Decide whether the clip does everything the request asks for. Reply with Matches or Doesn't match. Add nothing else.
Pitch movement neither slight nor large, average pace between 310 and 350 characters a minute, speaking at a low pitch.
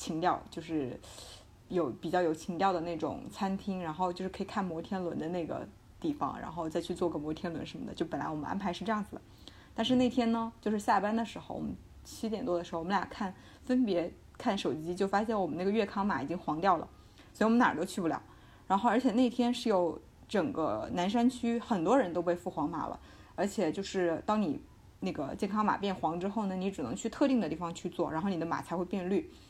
Doesn't match